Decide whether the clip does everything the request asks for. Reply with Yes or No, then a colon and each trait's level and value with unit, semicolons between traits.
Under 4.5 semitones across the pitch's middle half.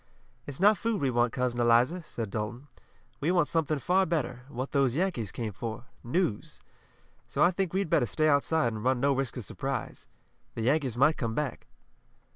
No: average, 5.1 semitones